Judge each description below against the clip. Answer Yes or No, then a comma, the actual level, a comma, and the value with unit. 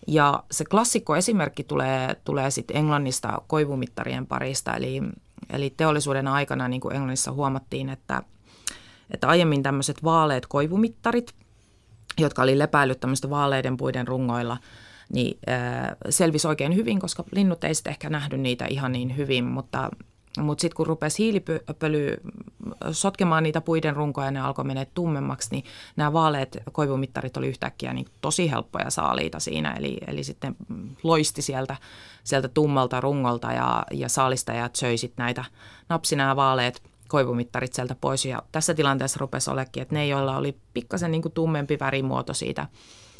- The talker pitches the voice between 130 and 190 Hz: Yes, low, 135 Hz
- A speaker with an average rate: Yes, average, 140 wpm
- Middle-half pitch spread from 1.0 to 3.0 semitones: No, average, 3.9 semitones